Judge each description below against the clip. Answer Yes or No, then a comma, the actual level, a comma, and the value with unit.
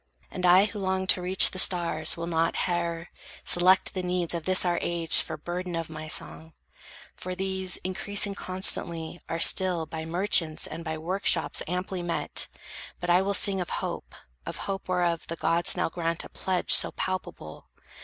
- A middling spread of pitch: No, narrow, 2.0 semitones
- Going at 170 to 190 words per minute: Yes, average, 180 wpm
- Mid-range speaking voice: Yes, medium, 175 Hz